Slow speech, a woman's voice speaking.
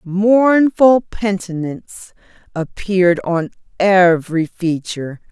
Yes: slow, 70 wpm; female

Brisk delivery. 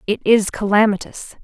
No: slow, 125 wpm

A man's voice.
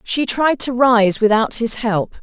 No: female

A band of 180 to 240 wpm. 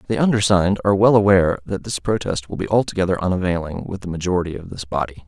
Yes: fast, 205 wpm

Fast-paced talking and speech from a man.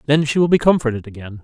Yes: fast, 250 wpm; male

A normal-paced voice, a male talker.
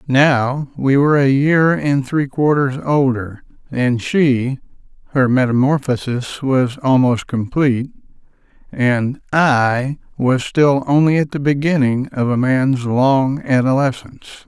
No: slow, 115 wpm; male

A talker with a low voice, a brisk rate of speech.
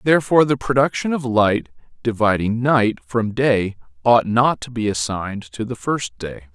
No: low, 115 Hz; average, 165 wpm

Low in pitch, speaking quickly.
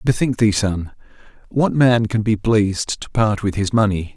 No: low, 105 Hz; average, 175 wpm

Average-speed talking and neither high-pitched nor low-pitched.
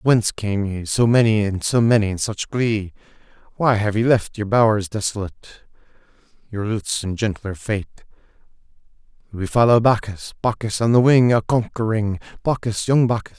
No: average, 155 wpm; low, 110 Hz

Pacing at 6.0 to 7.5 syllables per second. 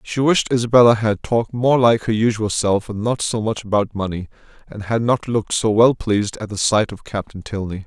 No: 5.4 syllables/s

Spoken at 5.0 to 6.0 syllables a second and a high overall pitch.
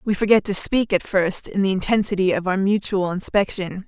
Yes: 5.3 syllables/s; high, 200 Hz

